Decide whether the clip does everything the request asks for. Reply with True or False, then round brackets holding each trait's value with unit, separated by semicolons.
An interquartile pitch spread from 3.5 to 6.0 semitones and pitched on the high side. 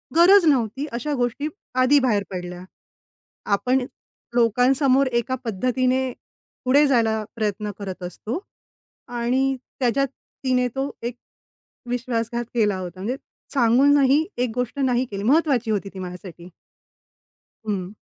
True (3.8 semitones; 245 Hz)